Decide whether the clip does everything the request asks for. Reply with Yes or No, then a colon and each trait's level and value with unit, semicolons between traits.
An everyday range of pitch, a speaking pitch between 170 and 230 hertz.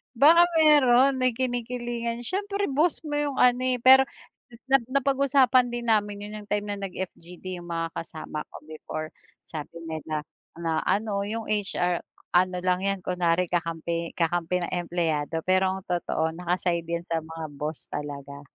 No: wide, 6.7 semitones; medium, 185 Hz